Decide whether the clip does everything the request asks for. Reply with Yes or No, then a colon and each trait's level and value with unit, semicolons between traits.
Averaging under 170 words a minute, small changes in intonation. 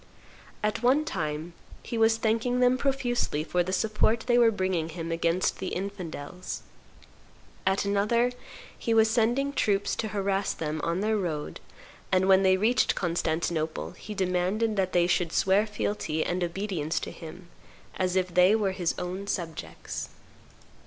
No: average, 150 wpm; average, 4.1 semitones